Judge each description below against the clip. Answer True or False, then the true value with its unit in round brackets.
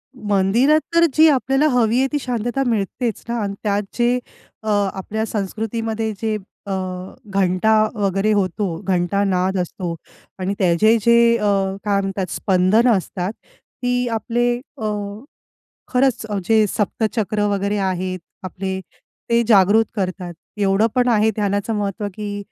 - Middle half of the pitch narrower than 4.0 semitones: True (3.2 semitones)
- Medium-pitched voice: False (210 Hz)